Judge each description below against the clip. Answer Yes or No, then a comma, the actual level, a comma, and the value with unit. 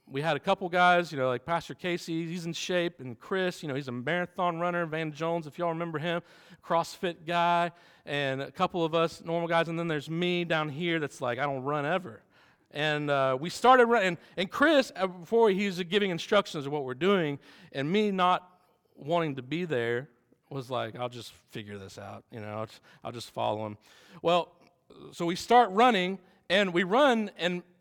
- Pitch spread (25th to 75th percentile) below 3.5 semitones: No, average, 4.0 semitones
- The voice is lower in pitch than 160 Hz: No, medium, 170 Hz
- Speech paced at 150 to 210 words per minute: Yes, fast, 205 wpm